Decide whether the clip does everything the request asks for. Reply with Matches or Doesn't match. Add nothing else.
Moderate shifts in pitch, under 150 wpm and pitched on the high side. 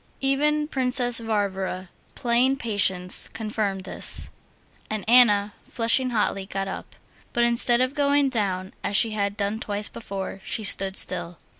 Matches